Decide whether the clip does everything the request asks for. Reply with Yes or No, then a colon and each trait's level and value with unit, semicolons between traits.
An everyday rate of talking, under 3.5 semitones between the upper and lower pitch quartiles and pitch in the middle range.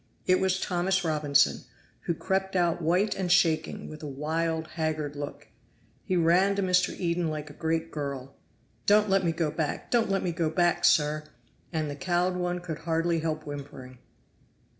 Yes: average, 175 wpm; average, 2.8 semitones; medium, 165 Hz